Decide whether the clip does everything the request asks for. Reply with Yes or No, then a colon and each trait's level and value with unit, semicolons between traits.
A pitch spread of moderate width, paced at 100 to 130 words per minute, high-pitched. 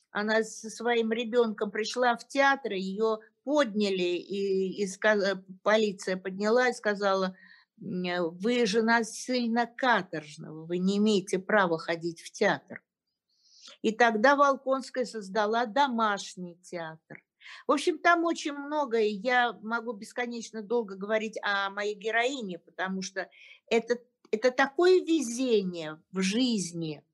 Yes: average, 4.0 semitones; average, 120 wpm; high, 220 Hz